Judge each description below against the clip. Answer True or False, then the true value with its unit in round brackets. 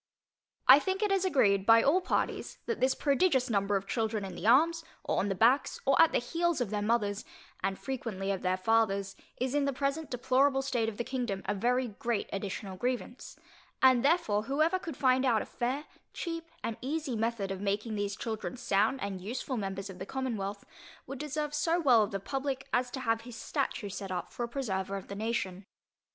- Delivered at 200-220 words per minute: True (205 wpm)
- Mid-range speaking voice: False (235 Hz)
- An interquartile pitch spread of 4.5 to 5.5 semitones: True (5.2 semitones)